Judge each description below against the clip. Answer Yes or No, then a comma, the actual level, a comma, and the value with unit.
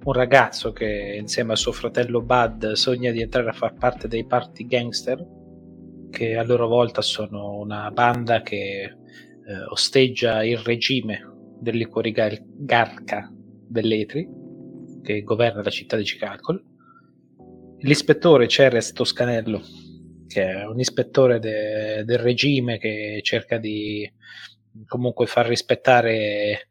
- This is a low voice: Yes, low, 115 Hz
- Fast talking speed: No, average, 120 wpm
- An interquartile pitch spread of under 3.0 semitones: Yes, narrow, 2.6 semitones